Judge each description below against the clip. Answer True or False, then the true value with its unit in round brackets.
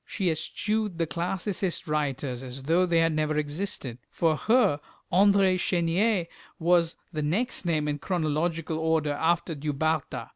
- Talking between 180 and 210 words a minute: False (145 wpm)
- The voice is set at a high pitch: False (165 Hz)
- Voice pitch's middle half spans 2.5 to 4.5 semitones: True (3.2 semitones)